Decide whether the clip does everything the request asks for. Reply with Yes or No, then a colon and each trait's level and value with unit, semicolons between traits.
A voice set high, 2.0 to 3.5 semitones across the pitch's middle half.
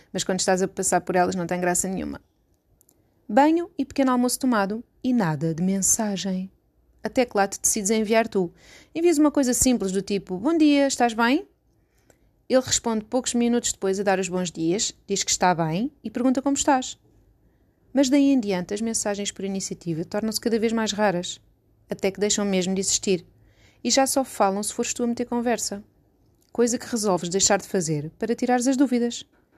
No: high, 215 Hz; average, 4.6 semitones